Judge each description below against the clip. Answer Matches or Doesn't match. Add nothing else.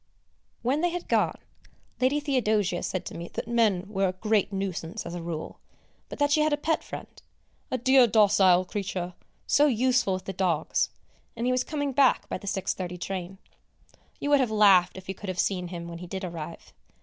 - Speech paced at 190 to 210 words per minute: Matches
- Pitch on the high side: Matches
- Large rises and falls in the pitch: Matches